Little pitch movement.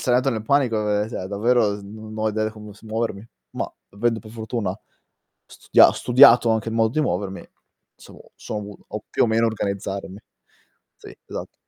Yes: narrow, 2.1 semitones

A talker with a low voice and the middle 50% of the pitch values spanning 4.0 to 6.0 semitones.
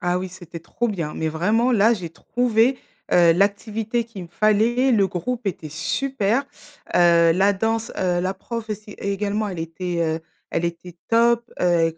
No: high, 200 Hz; average, 4.6 semitones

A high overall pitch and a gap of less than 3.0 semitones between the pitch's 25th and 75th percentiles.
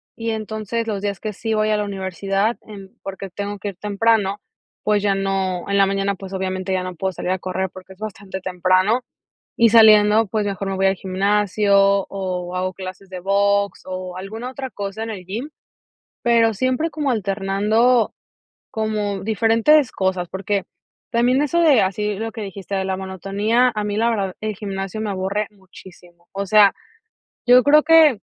Yes: high, 200 Hz; narrow, 2.4 semitones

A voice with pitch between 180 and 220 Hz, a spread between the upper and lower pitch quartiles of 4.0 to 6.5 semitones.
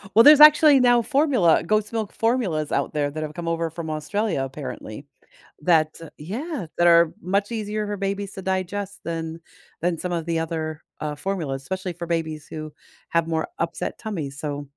No: medium, 170 Hz; average, 4.7 semitones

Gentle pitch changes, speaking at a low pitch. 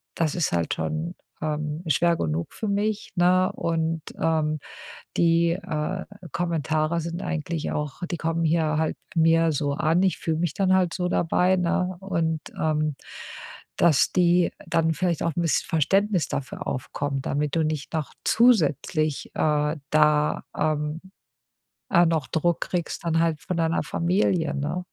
No: narrow, 2.2 semitones; medium, 165 Hz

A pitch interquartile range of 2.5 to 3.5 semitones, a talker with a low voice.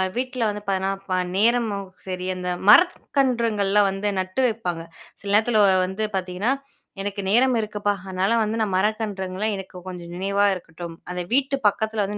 No: average, 2.8 semitones; high, 205 Hz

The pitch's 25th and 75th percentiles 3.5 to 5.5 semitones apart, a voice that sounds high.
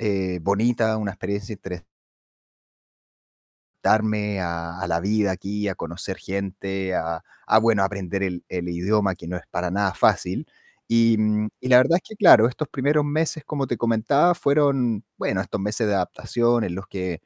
No: average, 3.9 semitones; low, 100 Hz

